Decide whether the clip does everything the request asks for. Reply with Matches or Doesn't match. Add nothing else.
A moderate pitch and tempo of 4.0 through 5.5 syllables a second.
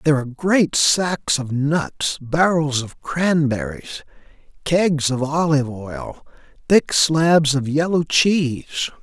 Doesn't match